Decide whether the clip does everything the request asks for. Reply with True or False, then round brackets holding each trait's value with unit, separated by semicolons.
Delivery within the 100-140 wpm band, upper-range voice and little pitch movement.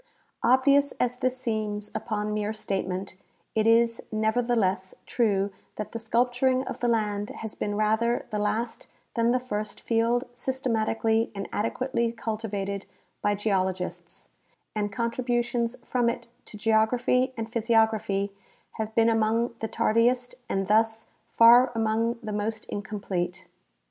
True (135 wpm; 225 Hz; 2.3 semitones)